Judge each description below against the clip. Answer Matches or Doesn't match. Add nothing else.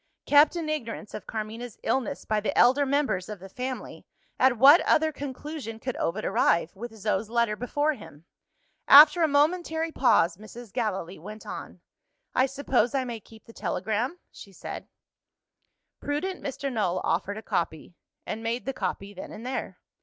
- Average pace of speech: Matches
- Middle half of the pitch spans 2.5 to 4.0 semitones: Doesn't match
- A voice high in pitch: Matches